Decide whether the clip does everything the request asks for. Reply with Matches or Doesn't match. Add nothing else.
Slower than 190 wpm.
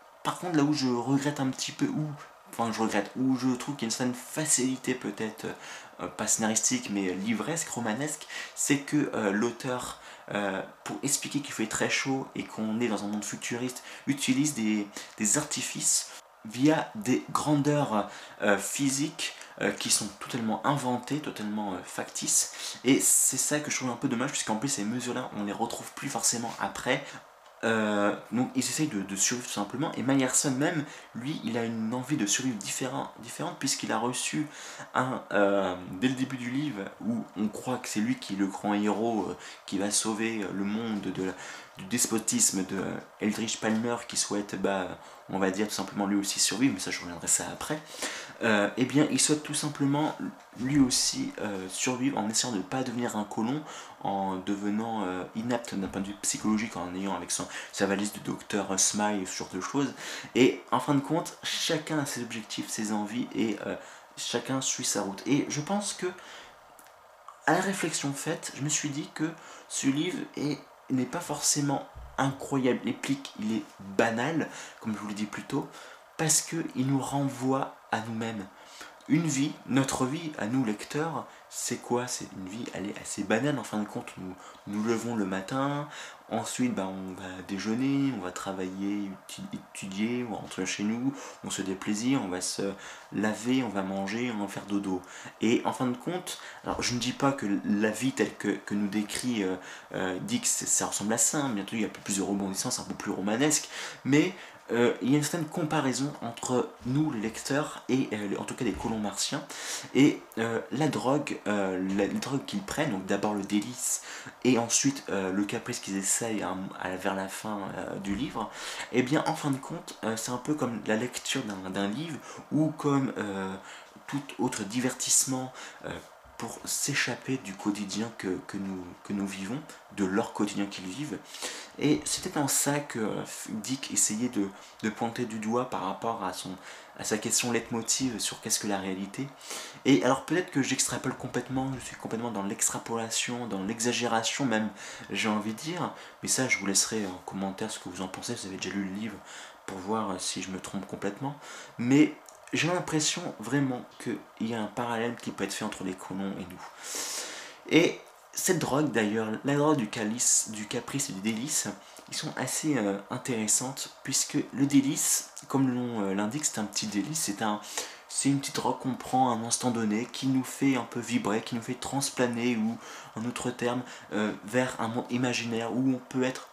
Doesn't match